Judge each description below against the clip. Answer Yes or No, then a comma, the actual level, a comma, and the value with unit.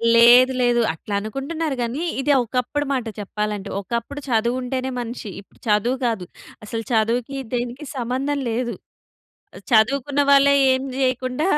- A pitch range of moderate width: Yes, average, 3.0 semitones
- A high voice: Yes, high, 245 Hz